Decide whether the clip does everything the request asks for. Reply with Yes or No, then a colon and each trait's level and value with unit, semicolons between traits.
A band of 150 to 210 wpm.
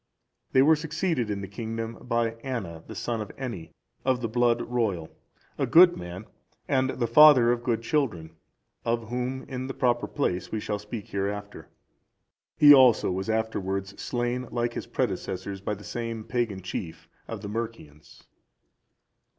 Yes: average, 160 wpm